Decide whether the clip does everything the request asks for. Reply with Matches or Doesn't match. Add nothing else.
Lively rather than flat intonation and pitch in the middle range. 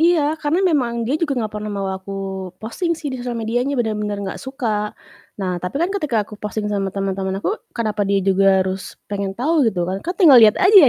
Doesn't match